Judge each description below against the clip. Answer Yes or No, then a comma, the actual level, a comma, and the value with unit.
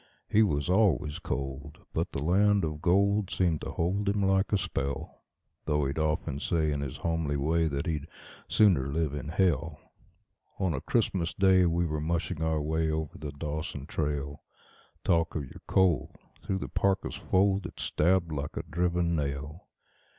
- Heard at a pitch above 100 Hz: No, very low, 80 Hz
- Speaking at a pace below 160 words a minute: No, average, 170 wpm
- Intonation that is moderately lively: Yes, average, 3.9 semitones